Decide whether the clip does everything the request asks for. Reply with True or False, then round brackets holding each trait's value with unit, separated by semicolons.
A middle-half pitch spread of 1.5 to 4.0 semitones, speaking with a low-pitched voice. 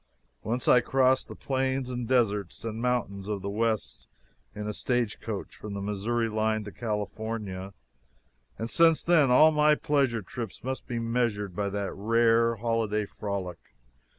True (3.2 semitones; 115 Hz)